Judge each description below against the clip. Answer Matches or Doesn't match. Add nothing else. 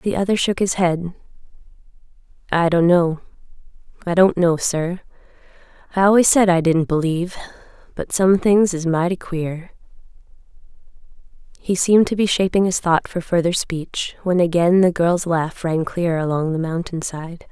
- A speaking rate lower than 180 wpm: Matches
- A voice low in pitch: Doesn't match